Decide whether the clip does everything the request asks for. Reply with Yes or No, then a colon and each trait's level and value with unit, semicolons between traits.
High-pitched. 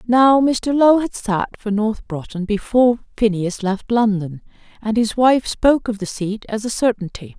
Yes: high, 220 Hz